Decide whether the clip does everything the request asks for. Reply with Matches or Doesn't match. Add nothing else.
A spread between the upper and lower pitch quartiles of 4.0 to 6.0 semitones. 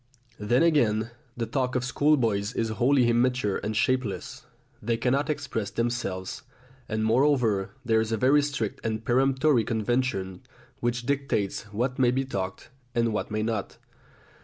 Doesn't match